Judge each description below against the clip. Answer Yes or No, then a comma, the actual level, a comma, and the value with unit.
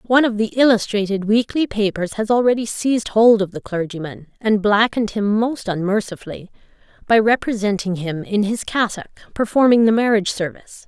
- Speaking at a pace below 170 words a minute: Yes, average, 155 wpm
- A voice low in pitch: No, high, 210 Hz